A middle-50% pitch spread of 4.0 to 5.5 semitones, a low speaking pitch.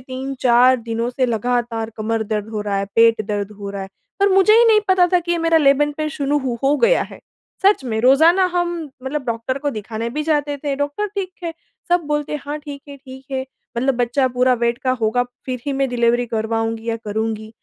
No: average, 4.5 semitones; very high, 260 Hz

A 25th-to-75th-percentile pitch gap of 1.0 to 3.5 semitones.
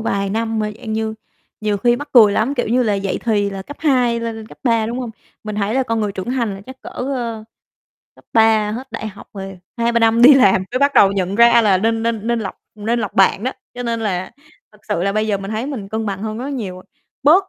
Yes: average, 2.8 semitones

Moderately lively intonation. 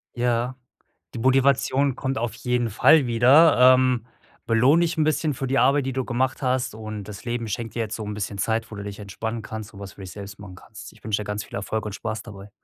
Yes: average, 3.8 semitones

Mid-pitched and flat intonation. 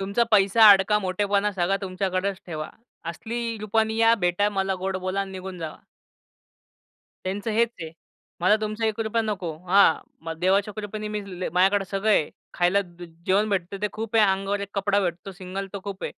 No: high, 195 Hz; narrow, 2.2 semitones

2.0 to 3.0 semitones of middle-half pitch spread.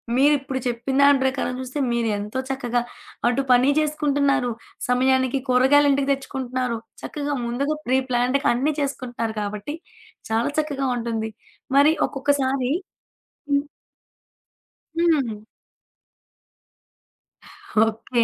Yes: average, 2.7 semitones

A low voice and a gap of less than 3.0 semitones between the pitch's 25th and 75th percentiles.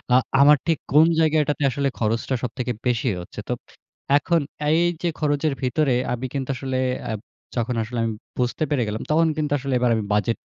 No: low, 130 Hz; average, 3.8 semitones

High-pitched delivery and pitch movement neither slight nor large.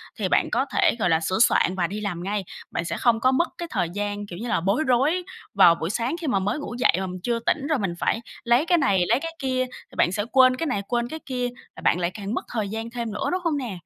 Yes: high, 230 Hz; average, 4.9 semitones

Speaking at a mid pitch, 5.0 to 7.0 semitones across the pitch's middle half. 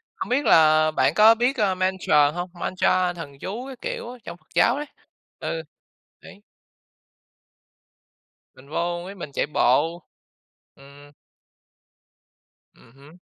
Yes: medium, 175 Hz; wide, 5.6 semitones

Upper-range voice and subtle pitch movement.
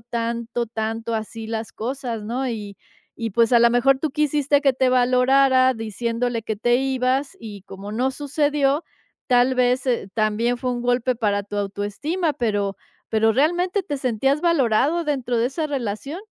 No: high, 245 Hz; average, 3.3 semitones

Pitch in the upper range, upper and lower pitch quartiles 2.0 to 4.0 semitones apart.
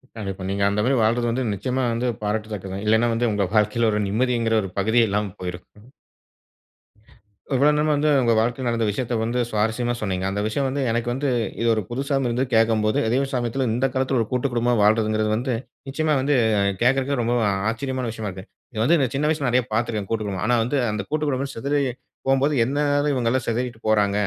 No: low, 120 Hz; average, 3.4 semitones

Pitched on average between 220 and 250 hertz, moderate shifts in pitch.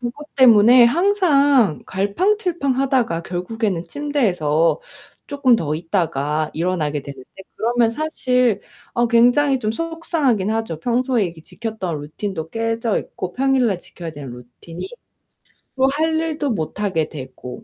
No: high, 225 Hz; wide, 8.1 semitones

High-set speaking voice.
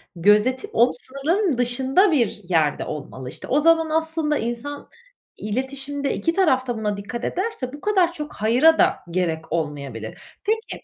Yes: very high, 260 Hz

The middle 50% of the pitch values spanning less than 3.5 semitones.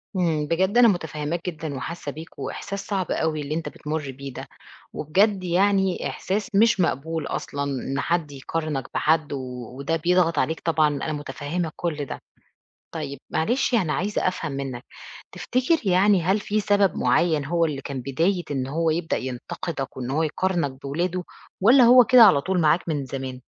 No: average, 4.6 semitones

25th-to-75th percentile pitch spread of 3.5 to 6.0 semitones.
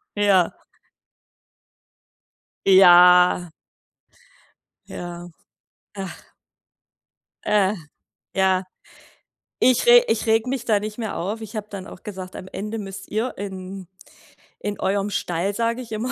No: average, 2.8 semitones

